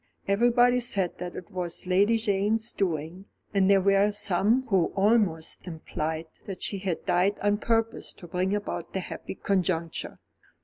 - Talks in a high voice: Yes, high, 195 Hz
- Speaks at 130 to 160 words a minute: Yes, average, 150 wpm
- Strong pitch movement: No, average, 2.7 semitones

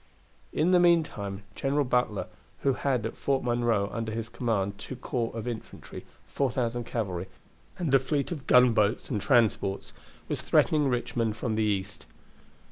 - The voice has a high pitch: No, low, 120 Hz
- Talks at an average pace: Yes, average, 150 wpm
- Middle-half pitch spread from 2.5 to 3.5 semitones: No, average, 3.9 semitones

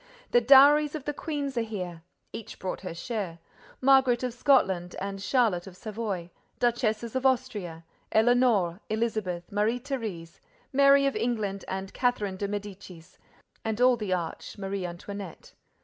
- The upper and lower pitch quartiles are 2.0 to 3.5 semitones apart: No, average, 4.8 semitones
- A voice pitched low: No, high, 215 Hz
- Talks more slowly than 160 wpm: Yes, average, 140 wpm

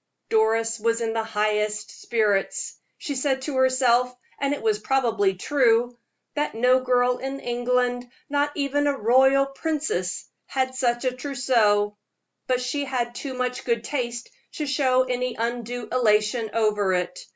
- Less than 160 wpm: Yes, average, 150 wpm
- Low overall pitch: No, high, 245 Hz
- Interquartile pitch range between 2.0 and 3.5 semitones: Yes, average, 2.8 semitones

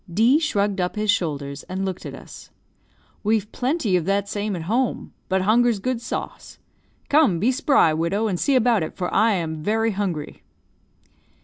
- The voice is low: No, high, 205 Hz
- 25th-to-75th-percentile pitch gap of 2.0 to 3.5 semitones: No, average, 4.3 semitones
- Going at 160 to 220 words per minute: Yes, average, 175 wpm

